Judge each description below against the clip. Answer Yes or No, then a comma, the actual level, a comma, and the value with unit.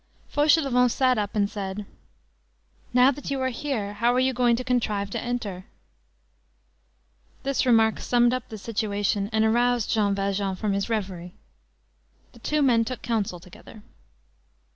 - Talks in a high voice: Yes, high, 225 Hz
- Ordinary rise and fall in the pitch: Yes, average, 3.7 semitones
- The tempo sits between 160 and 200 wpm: No, average, 150 wpm